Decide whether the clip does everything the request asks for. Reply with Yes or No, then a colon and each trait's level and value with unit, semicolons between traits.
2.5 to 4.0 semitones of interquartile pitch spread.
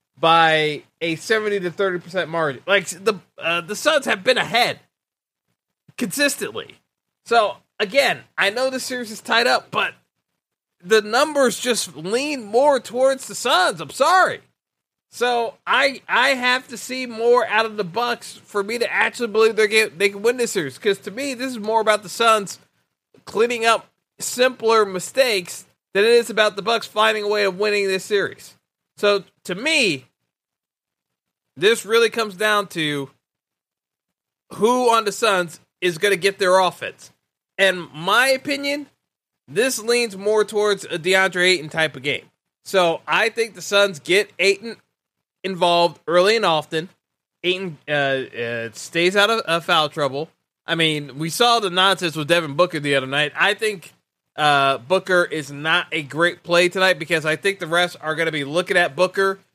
No: average, 4.9 semitones